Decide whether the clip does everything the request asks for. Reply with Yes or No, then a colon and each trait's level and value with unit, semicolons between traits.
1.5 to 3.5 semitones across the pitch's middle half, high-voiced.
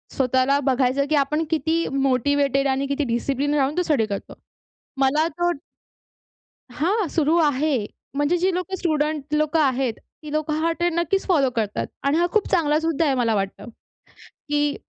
Yes: average, 3.2 semitones; very high, 290 Hz